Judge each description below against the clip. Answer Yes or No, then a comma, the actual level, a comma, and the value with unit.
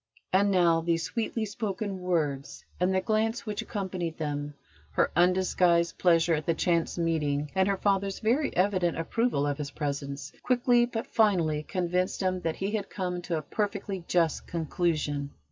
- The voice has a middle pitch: Yes, medium, 180 Hz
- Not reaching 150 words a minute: No, average, 160 wpm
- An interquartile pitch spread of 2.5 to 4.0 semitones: Yes, average, 3.6 semitones